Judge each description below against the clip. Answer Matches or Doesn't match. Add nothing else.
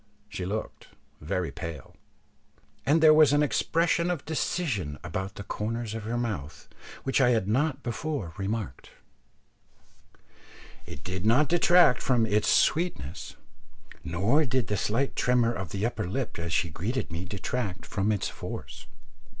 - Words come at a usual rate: Matches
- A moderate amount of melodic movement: Doesn't match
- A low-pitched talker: Matches